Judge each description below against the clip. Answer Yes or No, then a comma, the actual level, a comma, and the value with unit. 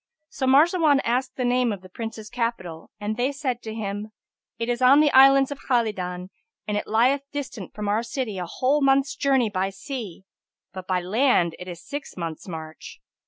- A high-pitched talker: Yes, high, 230 Hz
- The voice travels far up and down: Yes, wide, 5.7 semitones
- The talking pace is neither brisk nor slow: Yes, average, 190 wpm